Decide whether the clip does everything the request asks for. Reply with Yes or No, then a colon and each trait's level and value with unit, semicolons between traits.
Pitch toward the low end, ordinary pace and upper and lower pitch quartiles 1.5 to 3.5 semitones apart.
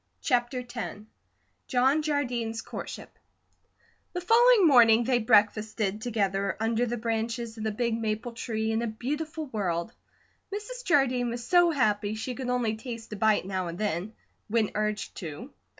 No: high, 230 Hz; average, 150 wpm; average, 2.8 semitones